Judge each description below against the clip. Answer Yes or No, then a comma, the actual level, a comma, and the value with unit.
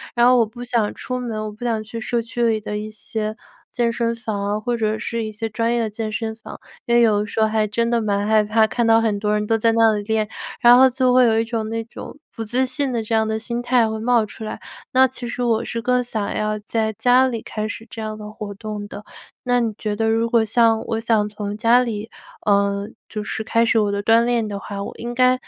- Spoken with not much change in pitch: Yes, narrow, 1.8 semitones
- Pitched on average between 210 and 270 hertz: Yes, high, 225 Hz